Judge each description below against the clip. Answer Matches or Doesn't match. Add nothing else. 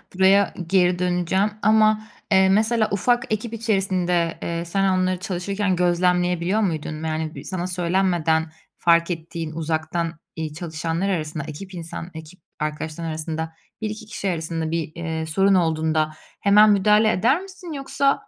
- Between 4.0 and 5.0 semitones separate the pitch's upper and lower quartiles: Doesn't match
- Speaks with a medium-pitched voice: Matches